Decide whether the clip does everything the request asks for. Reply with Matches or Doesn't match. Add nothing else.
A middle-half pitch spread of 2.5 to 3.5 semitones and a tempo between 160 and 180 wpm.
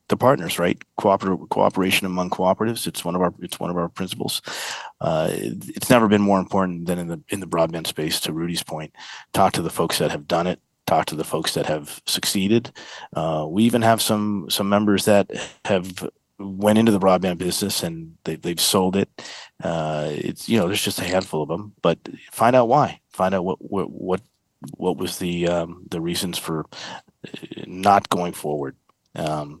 Doesn't match